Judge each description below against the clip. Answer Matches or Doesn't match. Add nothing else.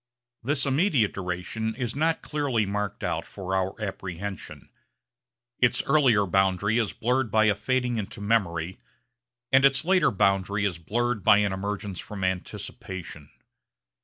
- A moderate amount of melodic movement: Matches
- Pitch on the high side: Doesn't match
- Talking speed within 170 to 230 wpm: Doesn't match